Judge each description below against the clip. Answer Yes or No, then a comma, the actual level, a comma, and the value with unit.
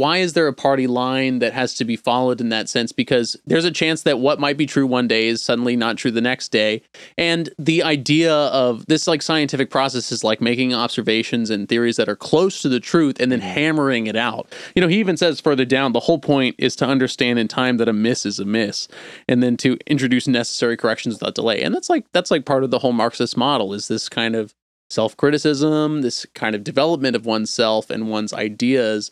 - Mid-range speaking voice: No, low, 125 Hz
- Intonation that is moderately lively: Yes, average, 4.2 semitones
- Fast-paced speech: Yes, fast, 230 wpm